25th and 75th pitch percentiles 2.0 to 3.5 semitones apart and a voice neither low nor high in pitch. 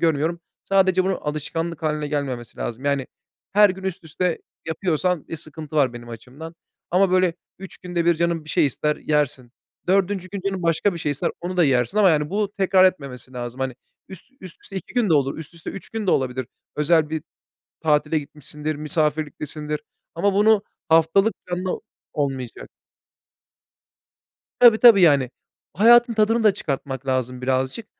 No: average, 4.7 semitones; medium, 160 Hz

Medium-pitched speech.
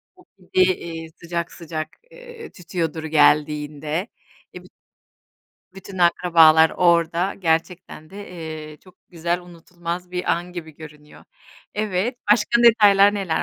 Yes: medium, 175 Hz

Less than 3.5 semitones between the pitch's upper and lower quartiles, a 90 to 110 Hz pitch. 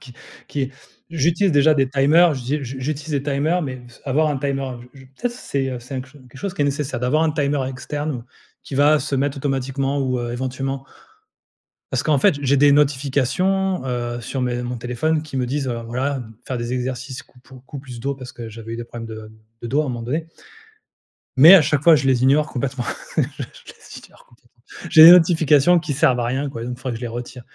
No: average, 2.9 semitones; low, 135 Hz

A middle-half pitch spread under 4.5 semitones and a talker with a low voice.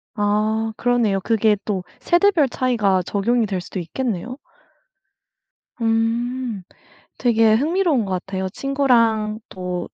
No: average, 3.7 semitones; high, 225 Hz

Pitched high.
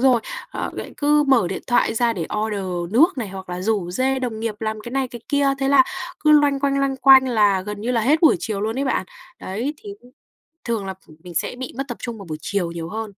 Yes: high, 230 Hz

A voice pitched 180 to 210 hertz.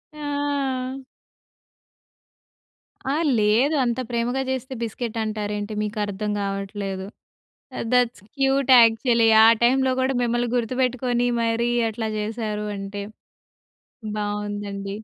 No: high, 225 Hz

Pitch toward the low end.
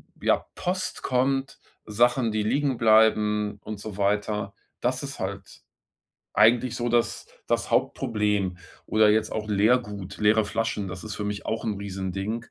Yes: low, 110 Hz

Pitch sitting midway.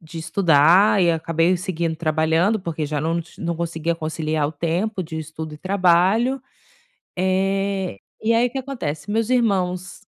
Yes: medium, 170 Hz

